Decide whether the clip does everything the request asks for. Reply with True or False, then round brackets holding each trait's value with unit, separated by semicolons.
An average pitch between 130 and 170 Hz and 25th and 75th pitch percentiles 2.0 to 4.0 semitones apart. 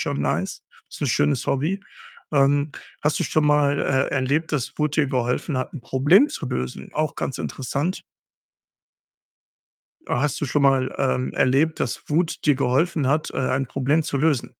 True (140 Hz; 2.8 semitones)